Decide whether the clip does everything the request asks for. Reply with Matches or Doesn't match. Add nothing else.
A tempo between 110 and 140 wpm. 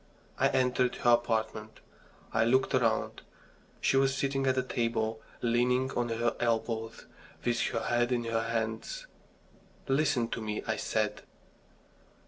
Matches